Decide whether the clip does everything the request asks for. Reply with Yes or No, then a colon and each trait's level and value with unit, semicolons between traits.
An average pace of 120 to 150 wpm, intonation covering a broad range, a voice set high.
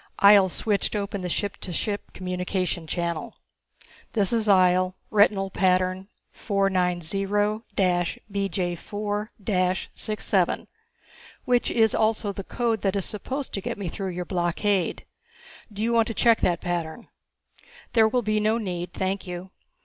No: slow, 135 wpm; average, 2.7 semitones; high, 195 Hz